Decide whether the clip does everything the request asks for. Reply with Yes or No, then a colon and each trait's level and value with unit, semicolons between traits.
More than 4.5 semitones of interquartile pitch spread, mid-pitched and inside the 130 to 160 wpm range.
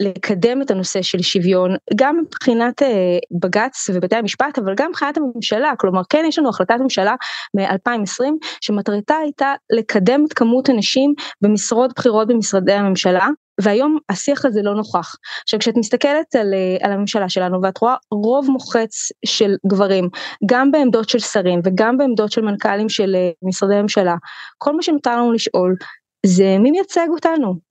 No: wide, 5.4 semitones; high, 220 Hz; fast, 150 wpm